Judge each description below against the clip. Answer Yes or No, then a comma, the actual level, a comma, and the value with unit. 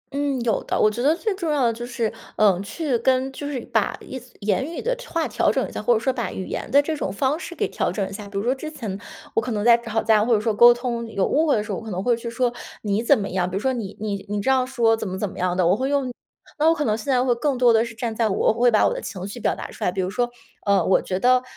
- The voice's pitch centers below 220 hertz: No, high, 235 Hz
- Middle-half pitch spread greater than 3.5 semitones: Yes, average, 4.1 semitones